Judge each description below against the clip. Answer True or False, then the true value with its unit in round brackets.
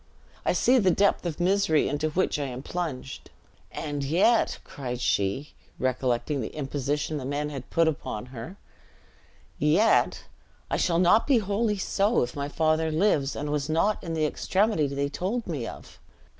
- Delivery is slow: False (170 wpm)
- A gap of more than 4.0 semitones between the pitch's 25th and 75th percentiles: True (4.9 semitones)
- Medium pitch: True (155 Hz)